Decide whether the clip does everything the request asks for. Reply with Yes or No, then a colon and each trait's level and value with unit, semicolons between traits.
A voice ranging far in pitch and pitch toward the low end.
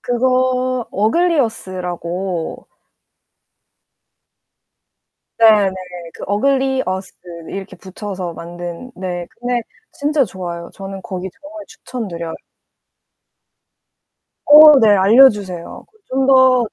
No: wide, 5.8 semitones; high, 210 Hz